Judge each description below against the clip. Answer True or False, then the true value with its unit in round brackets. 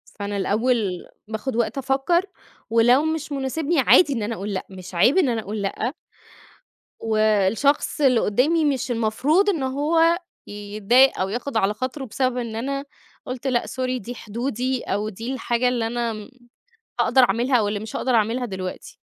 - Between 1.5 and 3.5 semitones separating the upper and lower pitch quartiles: False (4.0 semitones)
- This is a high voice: True (240 Hz)